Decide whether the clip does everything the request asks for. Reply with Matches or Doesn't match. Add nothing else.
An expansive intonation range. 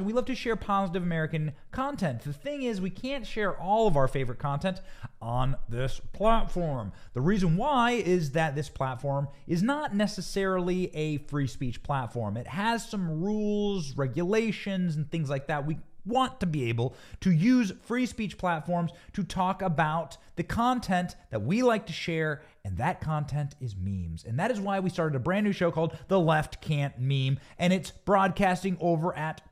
Matches